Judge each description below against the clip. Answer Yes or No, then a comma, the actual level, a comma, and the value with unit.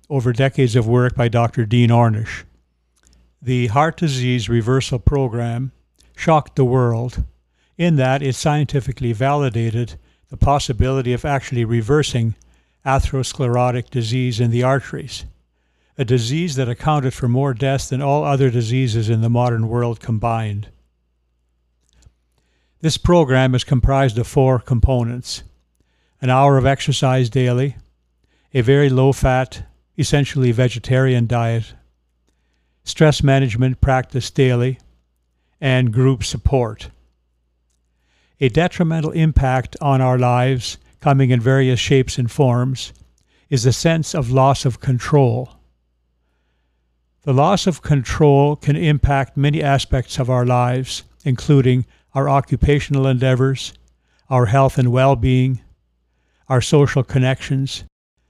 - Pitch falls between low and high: No, low, 125 Hz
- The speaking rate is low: Yes, slow, 120 wpm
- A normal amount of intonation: Yes, average, 5.0 semitones